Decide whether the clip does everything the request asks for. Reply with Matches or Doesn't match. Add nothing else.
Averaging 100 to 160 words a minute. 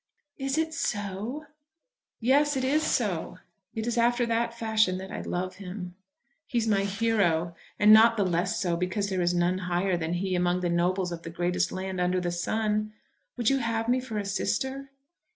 Doesn't match